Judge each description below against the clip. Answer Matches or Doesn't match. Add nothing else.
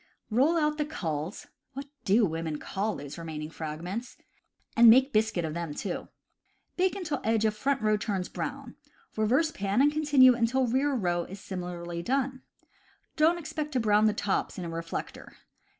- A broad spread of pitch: Matches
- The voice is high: Matches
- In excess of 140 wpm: Matches